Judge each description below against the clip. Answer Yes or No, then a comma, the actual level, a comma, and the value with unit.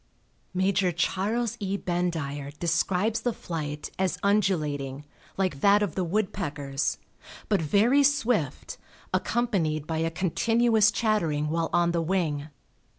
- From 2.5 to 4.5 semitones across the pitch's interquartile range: No, average, 5.0 semitones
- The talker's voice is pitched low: No, medium, 180 Hz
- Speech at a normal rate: No, slow, 120 wpm